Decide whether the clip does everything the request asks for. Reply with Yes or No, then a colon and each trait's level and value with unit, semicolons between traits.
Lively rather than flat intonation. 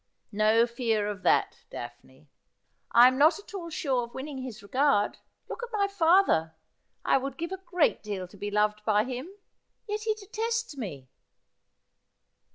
Yes: wide, 8.8 semitones